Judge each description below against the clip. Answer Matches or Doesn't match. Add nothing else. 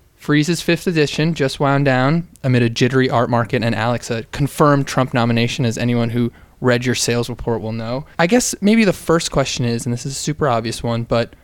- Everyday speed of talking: Doesn't match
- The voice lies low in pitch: Matches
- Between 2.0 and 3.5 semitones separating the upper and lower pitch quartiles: Doesn't match